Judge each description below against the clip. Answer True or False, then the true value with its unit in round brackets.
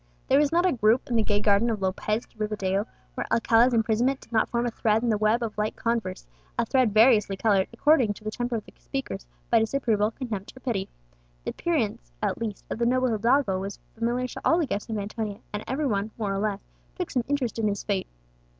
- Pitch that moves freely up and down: False (2.9 semitones)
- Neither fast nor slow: False (230 wpm)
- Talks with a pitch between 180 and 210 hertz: False (225 Hz)